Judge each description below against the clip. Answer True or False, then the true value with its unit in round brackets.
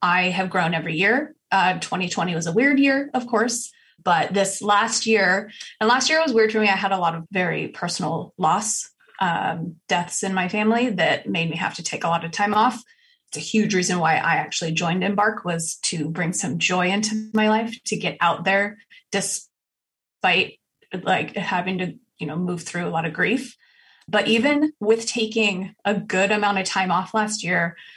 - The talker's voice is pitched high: True (195 Hz)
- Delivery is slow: False (200 wpm)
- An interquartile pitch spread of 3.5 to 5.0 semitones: True (4.1 semitones)